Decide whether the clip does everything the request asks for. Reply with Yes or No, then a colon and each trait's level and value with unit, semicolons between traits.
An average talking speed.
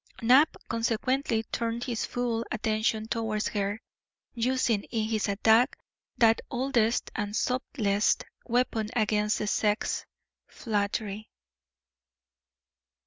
No: slow, 95 wpm